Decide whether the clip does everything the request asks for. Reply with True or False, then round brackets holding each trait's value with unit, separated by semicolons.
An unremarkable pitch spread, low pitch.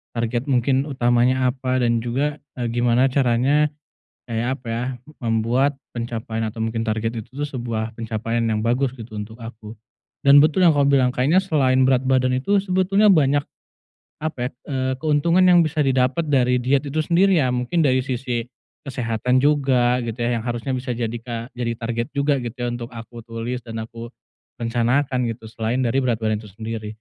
True (3.0 semitones; 125 Hz)